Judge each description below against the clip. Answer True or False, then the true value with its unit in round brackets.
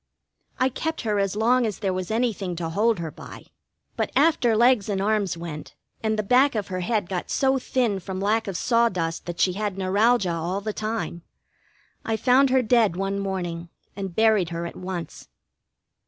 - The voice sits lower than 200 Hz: False (205 Hz)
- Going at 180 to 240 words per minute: True (185 wpm)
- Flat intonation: False (3.8 semitones)